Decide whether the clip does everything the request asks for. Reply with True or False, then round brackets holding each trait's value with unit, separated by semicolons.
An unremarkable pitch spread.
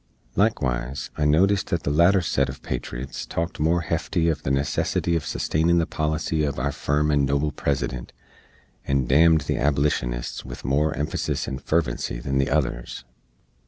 True (3.4 semitones)